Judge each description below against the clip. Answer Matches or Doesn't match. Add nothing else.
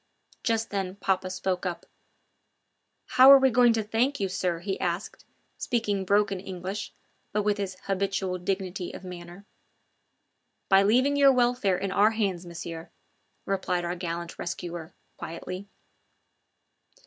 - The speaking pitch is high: Matches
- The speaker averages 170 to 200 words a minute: Doesn't match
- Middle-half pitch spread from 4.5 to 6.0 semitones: Doesn't match